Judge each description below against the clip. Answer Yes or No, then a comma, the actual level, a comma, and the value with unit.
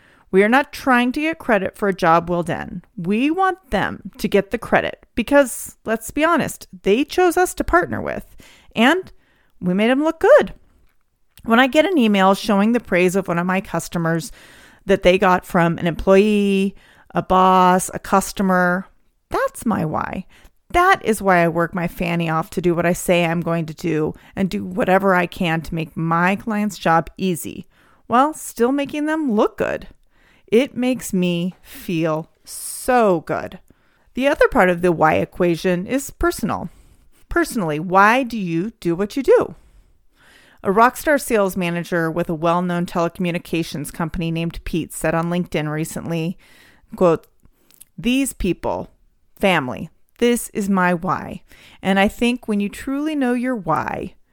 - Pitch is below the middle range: No, high, 195 Hz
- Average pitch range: No, wide, 5.9 semitones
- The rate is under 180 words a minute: Yes, average, 165 wpm